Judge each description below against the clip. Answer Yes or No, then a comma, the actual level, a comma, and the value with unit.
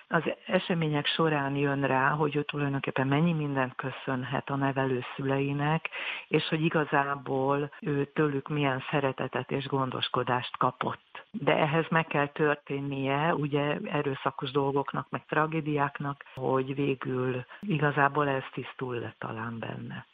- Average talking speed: Yes, average, 125 wpm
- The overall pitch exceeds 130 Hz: Yes, medium, 140 Hz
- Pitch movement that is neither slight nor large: No, narrow, 1.9 semitones